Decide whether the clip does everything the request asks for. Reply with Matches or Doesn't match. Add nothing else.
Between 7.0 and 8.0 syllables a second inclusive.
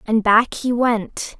Doesn't match